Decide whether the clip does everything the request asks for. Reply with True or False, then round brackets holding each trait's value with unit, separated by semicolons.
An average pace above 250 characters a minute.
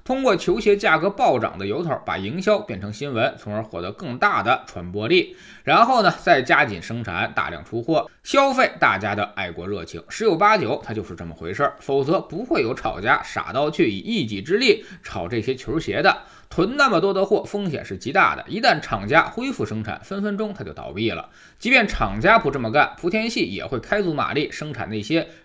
True (310 characters per minute)